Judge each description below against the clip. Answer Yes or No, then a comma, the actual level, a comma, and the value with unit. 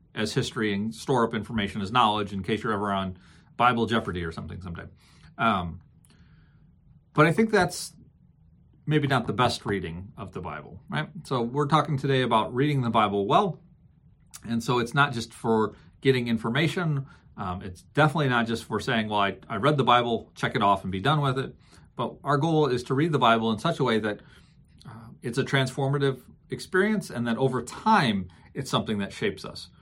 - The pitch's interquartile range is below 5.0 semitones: No, average, 5.3 semitones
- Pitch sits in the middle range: No, low, 120 Hz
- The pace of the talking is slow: No, average, 195 wpm